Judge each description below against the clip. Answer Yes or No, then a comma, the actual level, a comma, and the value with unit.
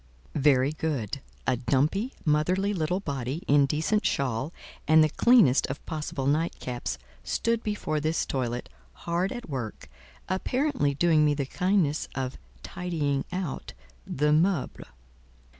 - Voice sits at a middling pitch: Yes, medium, 150 Hz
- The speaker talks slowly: Yes, slow, 125 wpm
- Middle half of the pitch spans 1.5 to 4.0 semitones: No, average, 4.8 semitones